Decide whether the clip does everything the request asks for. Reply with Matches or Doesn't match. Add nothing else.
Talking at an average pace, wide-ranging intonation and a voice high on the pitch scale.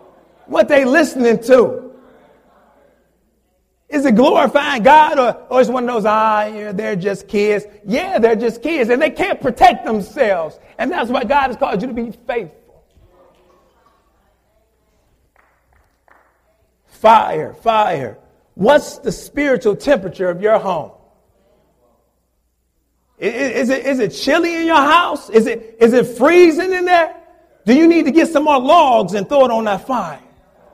Matches